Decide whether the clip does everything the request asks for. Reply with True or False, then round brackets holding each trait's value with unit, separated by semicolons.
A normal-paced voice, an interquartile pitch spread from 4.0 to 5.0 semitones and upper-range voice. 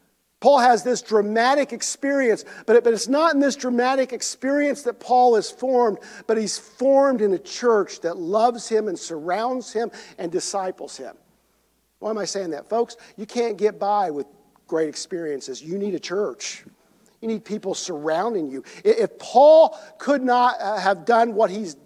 False (175 wpm; 3.5 semitones; 225 Hz)